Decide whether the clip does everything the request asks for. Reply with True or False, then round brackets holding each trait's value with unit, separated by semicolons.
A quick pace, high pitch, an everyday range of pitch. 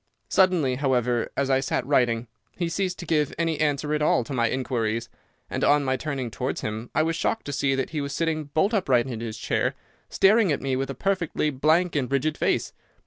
False (215 wpm; 140 Hz; 3.9 semitones)